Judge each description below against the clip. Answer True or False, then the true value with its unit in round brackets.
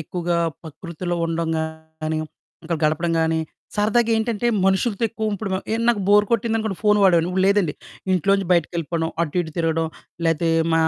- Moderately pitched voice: True (175 Hz)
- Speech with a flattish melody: False (4.2 semitones)